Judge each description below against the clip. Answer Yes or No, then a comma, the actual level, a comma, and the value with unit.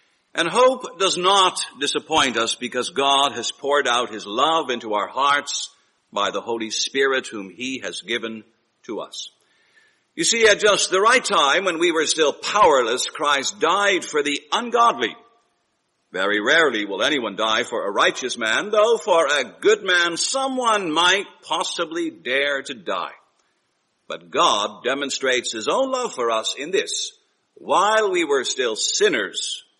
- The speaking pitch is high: Yes, high, 210 Hz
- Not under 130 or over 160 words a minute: Yes, average, 155 wpm